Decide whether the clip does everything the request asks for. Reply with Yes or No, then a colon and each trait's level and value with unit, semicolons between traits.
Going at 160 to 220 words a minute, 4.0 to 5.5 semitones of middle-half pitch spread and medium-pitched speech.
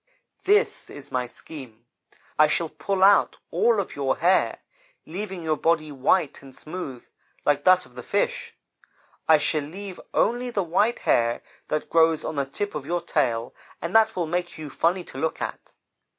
Yes: average, 175 wpm; average, 4.8 semitones; medium, 165 Hz